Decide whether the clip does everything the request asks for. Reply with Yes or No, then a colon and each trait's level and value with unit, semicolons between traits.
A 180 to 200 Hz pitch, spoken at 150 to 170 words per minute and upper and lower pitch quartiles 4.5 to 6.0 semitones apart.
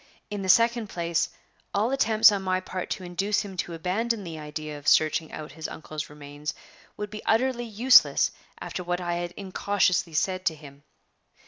No: medium, 185 Hz; average, 180 wpm; average, 4.8 semitones